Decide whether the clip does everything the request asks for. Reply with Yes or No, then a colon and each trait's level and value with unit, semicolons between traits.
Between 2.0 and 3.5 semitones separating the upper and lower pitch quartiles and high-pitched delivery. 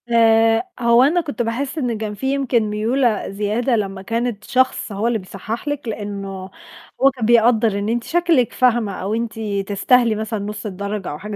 Yes: average, 3.0 semitones; high, 225 Hz